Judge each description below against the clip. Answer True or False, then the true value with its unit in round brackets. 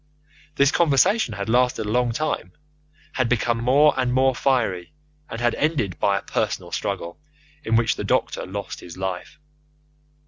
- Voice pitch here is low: True (120 Hz)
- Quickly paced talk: False (160 wpm)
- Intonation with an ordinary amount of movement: True (4.8 semitones)